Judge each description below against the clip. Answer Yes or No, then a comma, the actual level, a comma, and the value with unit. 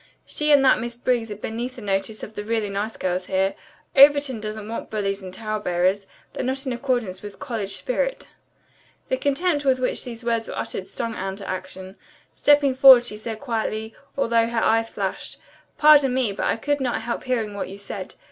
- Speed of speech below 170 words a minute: No, average, 200 wpm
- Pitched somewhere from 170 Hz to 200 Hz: No, high, 225 Hz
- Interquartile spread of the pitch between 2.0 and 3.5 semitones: No, average, 4.1 semitones